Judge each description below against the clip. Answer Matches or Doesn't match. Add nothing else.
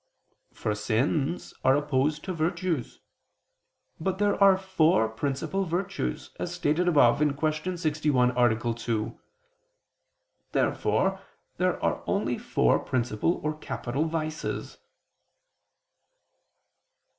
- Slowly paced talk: Matches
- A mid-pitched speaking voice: Matches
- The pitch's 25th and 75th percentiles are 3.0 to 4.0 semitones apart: Doesn't match